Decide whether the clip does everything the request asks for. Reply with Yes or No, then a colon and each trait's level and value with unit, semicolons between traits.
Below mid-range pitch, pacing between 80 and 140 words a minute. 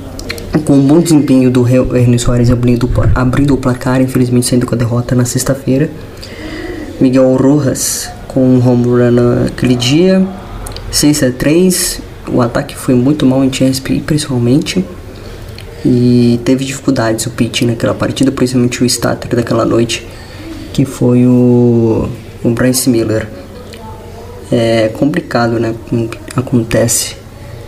Yes: low, 125 Hz; average, 125 wpm